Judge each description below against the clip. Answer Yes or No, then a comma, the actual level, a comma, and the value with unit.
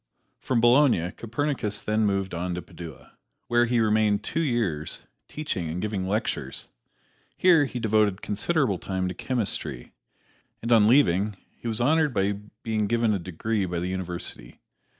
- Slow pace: No, average, 150 wpm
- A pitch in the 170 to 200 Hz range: No, low, 105 Hz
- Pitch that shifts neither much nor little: Yes, average, 4.3 semitones